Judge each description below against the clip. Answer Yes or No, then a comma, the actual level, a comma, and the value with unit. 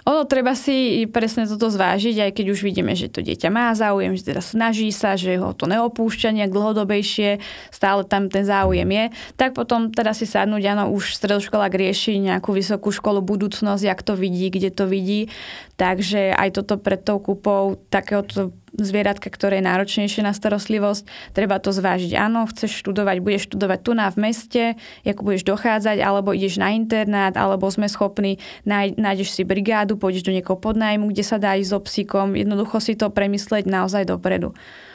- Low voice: No, high, 205 Hz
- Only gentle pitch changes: Yes, narrow, 1.6 semitones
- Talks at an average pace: No, fast, 175 wpm